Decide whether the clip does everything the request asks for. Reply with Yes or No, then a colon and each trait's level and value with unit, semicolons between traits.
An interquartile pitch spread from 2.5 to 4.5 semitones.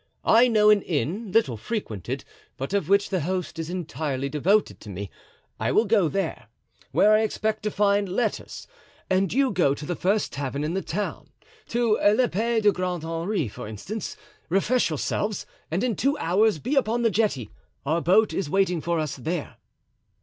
No: average, 5.2 semitones